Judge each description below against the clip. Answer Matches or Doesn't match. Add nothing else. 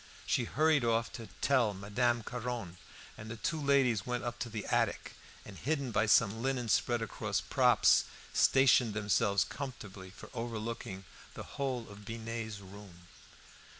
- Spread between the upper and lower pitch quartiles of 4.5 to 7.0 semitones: Doesn't match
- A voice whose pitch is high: Doesn't match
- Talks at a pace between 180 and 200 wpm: Doesn't match